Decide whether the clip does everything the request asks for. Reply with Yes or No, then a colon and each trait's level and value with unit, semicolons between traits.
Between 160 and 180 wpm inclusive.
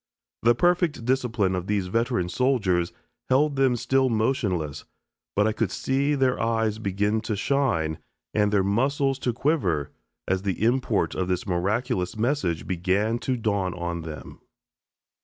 No: average, 145 wpm